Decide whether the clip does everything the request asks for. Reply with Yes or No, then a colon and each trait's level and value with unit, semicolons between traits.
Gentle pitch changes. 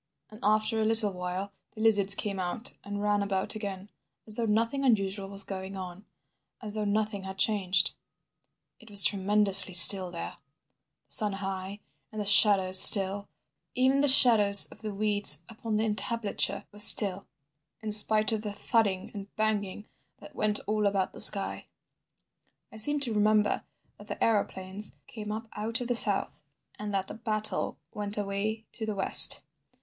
Yes: narrow, 1.8 semitones